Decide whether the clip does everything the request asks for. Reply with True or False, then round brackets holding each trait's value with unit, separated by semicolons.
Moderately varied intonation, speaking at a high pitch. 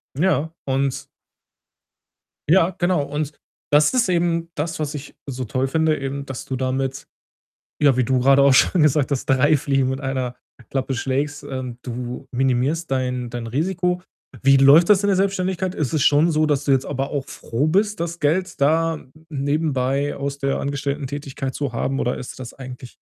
False (3.2 semitones; 140 Hz)